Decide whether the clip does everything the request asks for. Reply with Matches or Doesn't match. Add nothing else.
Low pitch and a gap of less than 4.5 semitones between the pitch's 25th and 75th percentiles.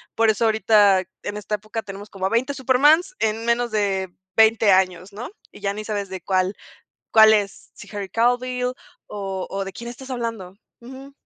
Doesn't match